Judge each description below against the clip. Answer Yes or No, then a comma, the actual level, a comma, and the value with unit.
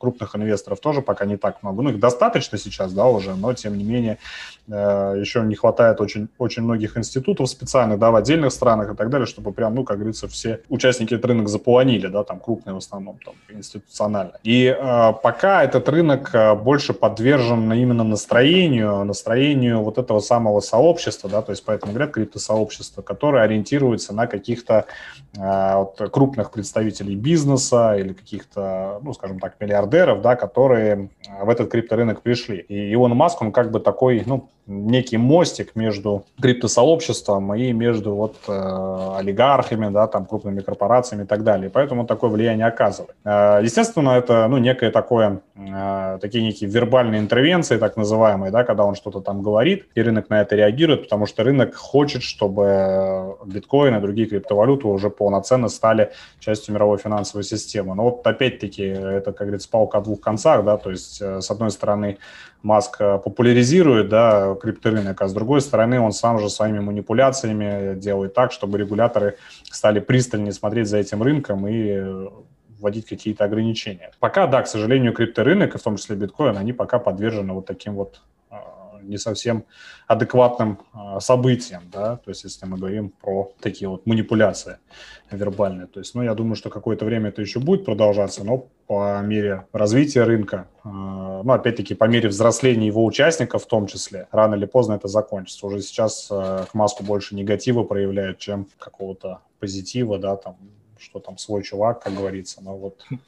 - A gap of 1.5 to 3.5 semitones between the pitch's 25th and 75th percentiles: Yes, average, 3.0 semitones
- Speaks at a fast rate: Yes, fast, 165 wpm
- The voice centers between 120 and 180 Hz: No, low, 105 Hz